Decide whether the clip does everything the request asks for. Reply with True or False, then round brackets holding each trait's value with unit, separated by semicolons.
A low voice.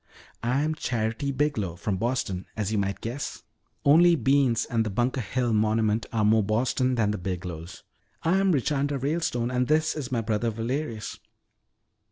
True (120 Hz)